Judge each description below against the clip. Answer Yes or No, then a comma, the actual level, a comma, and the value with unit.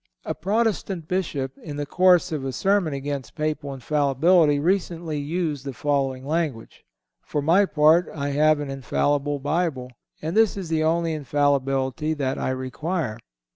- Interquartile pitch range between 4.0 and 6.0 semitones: No, average, 3.4 semitones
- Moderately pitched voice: Yes, medium, 150 Hz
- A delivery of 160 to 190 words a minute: No, average, 150 wpm